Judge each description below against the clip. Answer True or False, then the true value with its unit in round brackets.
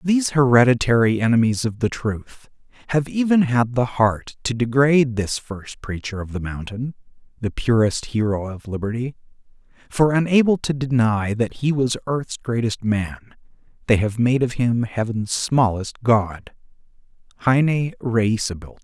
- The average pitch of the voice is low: True (120 Hz)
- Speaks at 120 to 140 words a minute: True (135 wpm)